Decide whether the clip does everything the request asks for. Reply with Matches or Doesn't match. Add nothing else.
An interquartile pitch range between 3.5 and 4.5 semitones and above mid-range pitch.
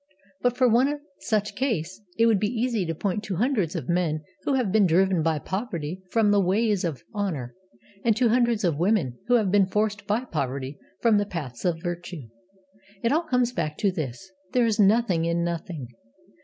Doesn't match